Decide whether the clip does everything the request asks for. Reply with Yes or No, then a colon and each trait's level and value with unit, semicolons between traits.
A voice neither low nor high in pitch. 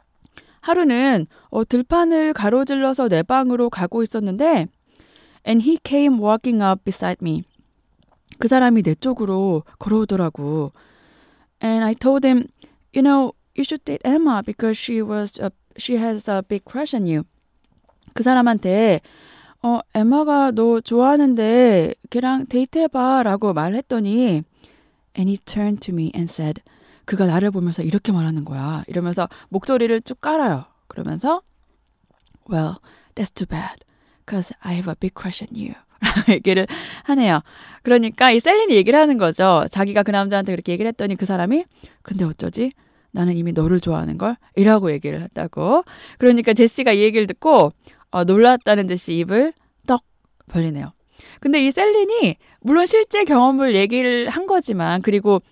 No: high, 220 Hz